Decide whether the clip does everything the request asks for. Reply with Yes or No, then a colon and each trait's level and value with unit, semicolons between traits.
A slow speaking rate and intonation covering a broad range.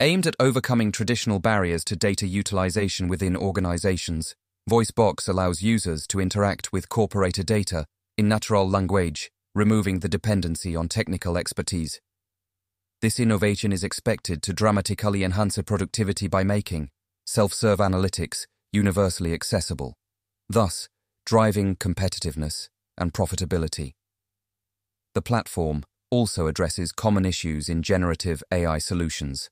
No: slow, 115 wpm; average, 2.7 semitones